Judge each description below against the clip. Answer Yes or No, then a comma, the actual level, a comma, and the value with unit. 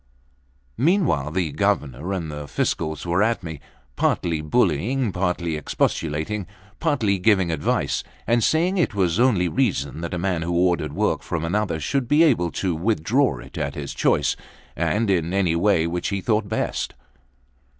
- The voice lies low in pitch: Yes, very low, 90 Hz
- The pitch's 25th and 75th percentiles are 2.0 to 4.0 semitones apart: No, average, 5.3 semitones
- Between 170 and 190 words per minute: No, average, 160 wpm